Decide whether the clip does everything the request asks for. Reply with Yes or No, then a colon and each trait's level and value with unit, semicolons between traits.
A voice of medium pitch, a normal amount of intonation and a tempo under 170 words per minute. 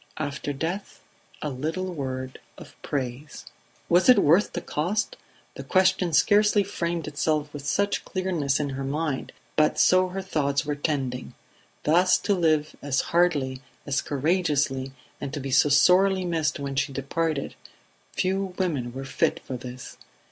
Yes: medium, 150 Hz; average, 4.6 semitones; average, 150 wpm